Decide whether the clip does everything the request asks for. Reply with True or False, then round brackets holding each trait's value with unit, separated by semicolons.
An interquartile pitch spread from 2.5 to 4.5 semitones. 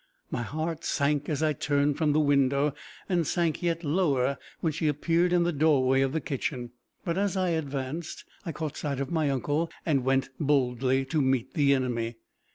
True (3.3 semitones)